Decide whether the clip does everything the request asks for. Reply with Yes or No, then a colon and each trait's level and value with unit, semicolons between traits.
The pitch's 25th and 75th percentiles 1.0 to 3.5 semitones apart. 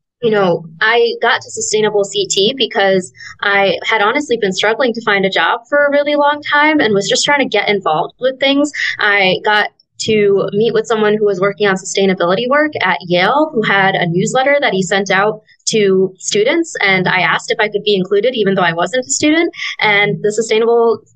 No: average, 4.3 semitones